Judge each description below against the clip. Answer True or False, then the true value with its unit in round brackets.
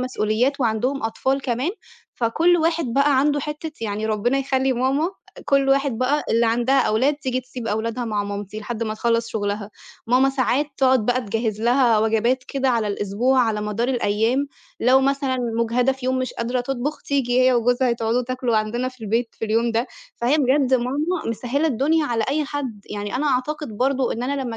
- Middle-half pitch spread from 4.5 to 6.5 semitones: False (3.2 semitones)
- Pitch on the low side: False (250 Hz)